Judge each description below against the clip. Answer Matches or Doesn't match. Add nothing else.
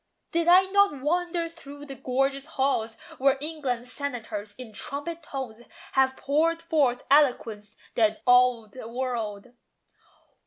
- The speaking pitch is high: Matches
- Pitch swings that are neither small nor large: Matches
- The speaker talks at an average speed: Doesn't match